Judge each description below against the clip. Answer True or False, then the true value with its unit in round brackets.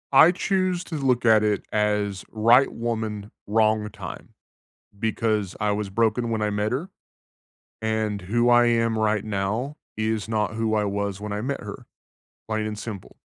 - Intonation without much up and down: True (1.9 semitones)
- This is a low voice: True (110 Hz)